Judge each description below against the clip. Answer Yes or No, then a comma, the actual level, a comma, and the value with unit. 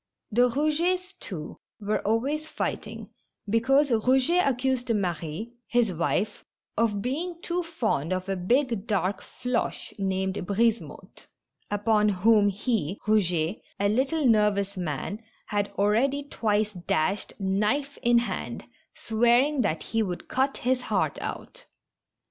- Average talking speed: No, slow, 125 wpm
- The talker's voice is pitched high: Yes, high, 220 Hz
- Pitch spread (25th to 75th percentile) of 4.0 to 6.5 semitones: Yes, average, 4.7 semitones